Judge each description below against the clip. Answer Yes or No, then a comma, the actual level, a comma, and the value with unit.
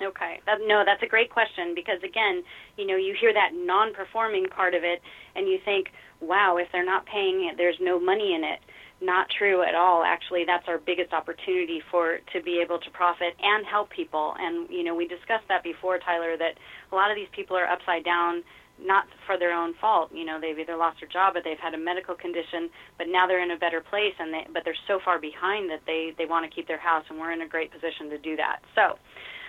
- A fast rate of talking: Yes, fast, 235 wpm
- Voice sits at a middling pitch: Yes, medium, 175 Hz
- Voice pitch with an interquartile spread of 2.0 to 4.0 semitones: Yes, average, 3.1 semitones